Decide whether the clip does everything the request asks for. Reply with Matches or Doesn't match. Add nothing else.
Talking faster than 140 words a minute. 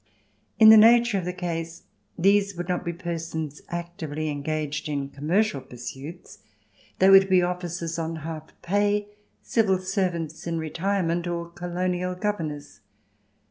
Doesn't match